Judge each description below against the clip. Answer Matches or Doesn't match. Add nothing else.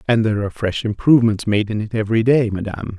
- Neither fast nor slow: Doesn't match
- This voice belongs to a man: Matches